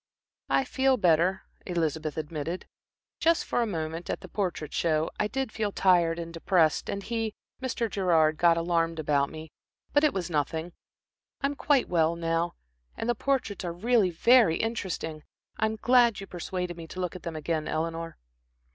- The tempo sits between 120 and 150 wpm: No, average, 175 wpm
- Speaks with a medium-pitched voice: Yes, medium, 175 Hz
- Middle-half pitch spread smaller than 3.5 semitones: No, average, 5.0 semitones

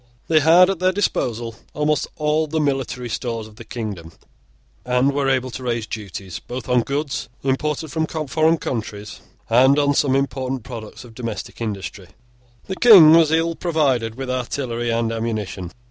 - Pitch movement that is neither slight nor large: Yes, average, 4.9 semitones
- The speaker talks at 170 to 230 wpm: No, average, 160 wpm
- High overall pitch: No, low, 130 Hz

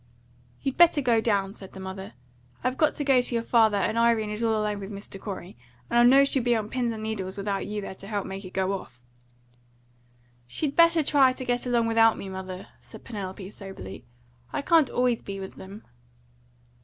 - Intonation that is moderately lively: Yes, average, 4.1 semitones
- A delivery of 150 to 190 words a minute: No, fast, 205 wpm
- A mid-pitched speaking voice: No, high, 220 Hz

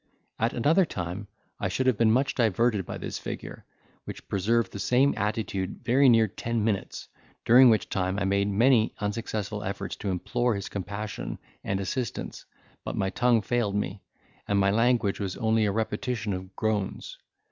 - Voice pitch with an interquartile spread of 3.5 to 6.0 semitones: No, average, 3.1 semitones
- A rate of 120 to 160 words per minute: No, average, 170 wpm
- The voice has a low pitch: Yes, low, 105 Hz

